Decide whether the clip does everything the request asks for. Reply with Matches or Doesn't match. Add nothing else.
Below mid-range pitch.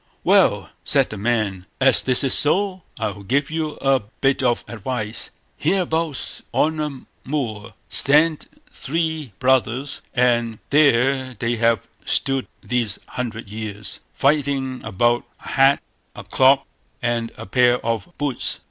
Matches